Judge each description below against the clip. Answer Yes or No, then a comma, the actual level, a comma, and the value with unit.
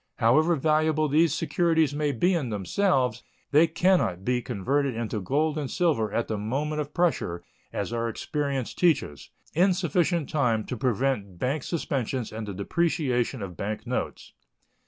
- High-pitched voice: No, medium, 140 Hz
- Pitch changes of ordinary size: No, wide, 5.8 semitones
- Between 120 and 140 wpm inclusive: No, average, 155 wpm